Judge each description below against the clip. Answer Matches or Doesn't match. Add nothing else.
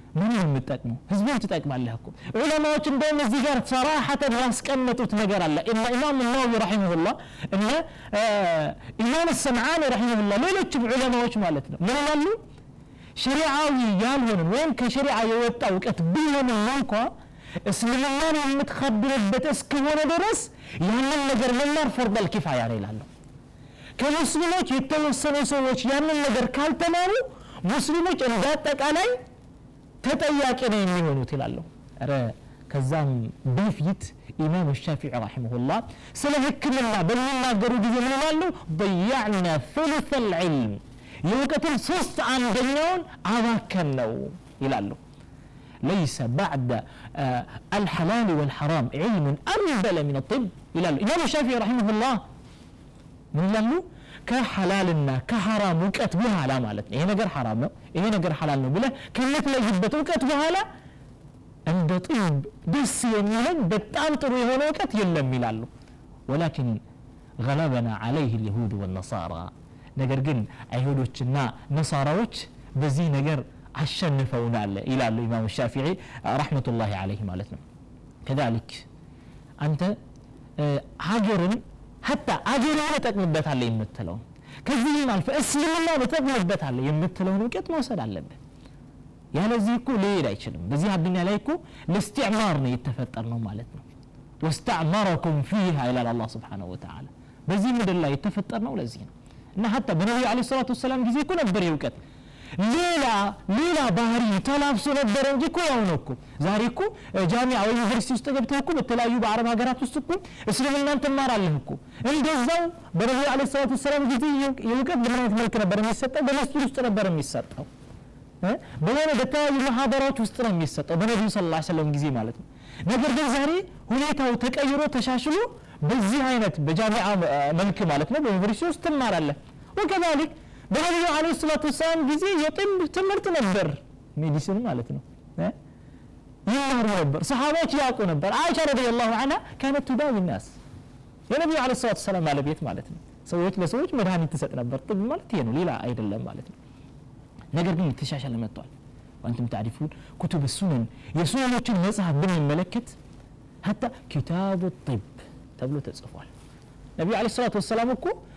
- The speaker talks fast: Matches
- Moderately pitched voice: Doesn't match